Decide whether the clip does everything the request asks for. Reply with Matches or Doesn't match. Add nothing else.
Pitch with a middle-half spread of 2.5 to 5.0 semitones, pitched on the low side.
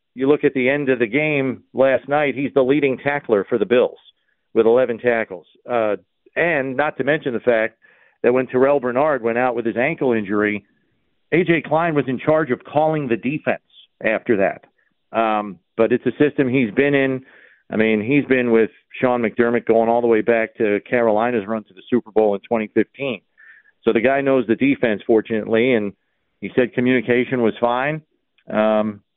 Matches